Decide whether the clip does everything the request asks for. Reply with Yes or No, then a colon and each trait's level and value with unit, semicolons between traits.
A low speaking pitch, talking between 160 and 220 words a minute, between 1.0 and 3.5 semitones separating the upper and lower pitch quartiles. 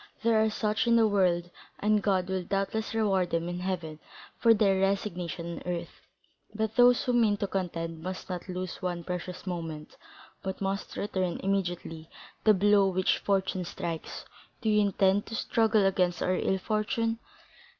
No: high, 190 Hz; average, 165 wpm; average, 2.9 semitones